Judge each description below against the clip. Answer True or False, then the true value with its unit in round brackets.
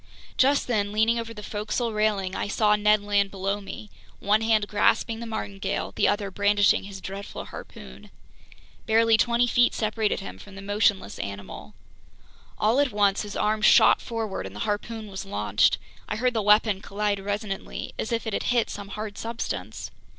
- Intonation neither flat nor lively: False (2.0 semitones)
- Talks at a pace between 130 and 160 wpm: False (175 wpm)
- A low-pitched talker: False (210 Hz)